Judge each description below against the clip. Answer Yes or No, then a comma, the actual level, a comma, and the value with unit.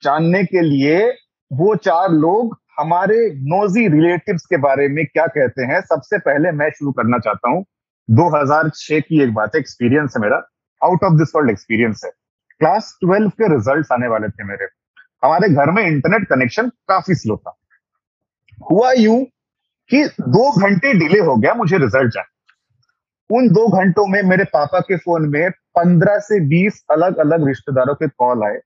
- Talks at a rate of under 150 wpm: No, average, 170 wpm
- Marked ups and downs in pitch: Yes, wide, 6.1 semitones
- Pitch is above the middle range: No, medium, 165 Hz